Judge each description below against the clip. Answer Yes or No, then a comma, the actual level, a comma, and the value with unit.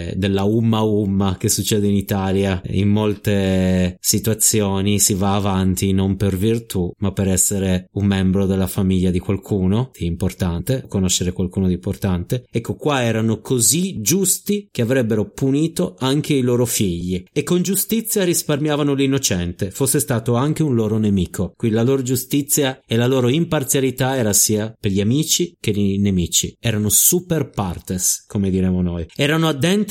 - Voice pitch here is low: Yes, low, 105 Hz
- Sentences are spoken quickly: No, average, 155 wpm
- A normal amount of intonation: No, wide, 5.7 semitones